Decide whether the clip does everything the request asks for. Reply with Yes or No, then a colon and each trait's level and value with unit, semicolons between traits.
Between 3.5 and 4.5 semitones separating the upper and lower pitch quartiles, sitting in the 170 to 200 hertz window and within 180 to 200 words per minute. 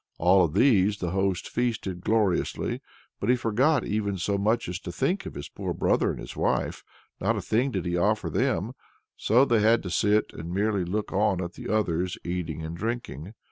No: average, 3.8 semitones; low, 100 Hz; average, 195 wpm